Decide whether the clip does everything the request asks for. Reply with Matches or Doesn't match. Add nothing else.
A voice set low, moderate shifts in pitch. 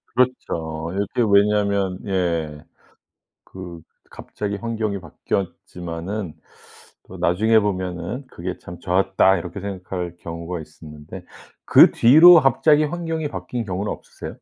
Matches